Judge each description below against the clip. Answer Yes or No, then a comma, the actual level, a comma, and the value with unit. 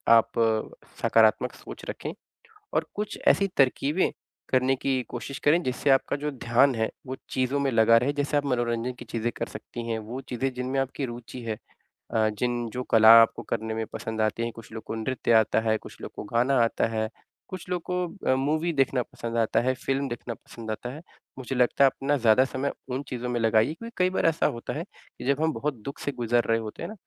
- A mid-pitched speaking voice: No, low, 125 Hz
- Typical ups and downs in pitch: Yes, average, 3.2 semitones